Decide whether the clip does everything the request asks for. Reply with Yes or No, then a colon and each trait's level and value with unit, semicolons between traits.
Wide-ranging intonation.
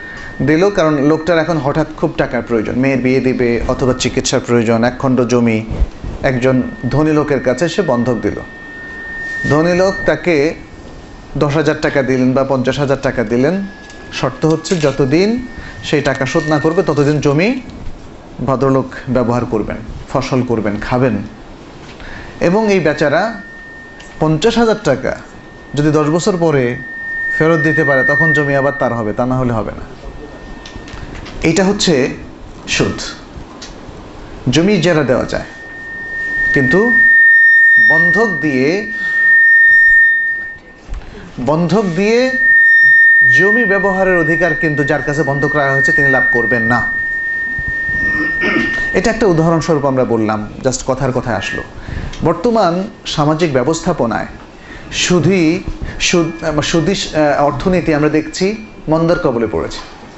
Yes: wide, 7.6 semitones